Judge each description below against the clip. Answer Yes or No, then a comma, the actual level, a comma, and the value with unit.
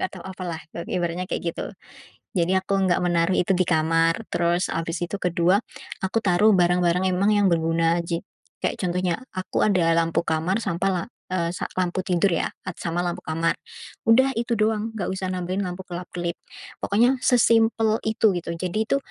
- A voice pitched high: No, medium, 180 Hz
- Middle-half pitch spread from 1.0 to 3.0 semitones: Yes, average, 2.7 semitones